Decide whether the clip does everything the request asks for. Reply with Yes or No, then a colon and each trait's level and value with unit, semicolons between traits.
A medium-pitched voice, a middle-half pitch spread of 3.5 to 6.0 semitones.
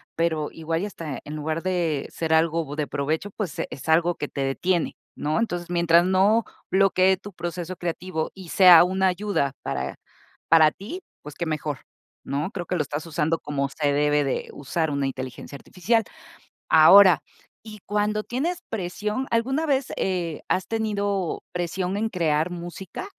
Yes: medium, 175 Hz; average, 4.1 semitones